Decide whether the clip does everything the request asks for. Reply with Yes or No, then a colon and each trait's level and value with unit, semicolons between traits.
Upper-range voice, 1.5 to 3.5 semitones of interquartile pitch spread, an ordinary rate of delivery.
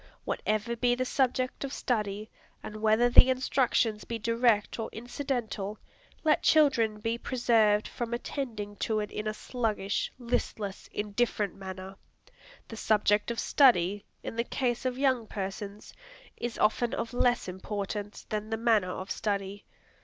Yes: high, 220 Hz; average, 2.8 semitones; average, 145 wpm